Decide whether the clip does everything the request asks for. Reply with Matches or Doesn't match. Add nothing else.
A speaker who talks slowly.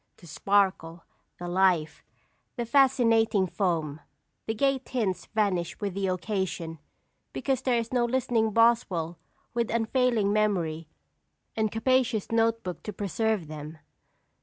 Matches